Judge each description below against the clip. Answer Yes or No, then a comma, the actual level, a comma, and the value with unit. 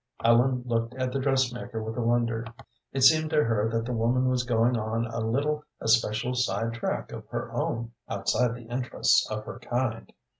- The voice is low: Yes, low, 120 Hz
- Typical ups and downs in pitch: No, narrow, 2.0 semitones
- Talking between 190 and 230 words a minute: No, average, 180 wpm